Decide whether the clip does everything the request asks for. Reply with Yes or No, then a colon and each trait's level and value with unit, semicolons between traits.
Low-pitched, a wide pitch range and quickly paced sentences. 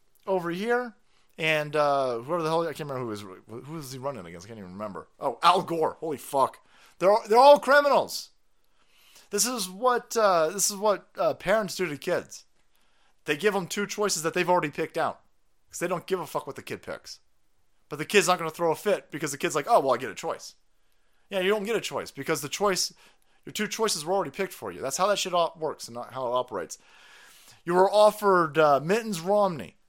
No: medium, 180 Hz; wide, 5.9 semitones; fast, 230 wpm